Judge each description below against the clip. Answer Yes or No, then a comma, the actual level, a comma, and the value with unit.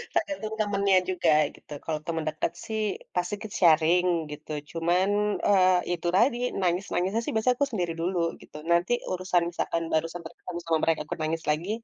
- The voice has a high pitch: No, medium, 180 Hz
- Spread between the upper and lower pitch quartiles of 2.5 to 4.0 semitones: Yes, average, 3.2 semitones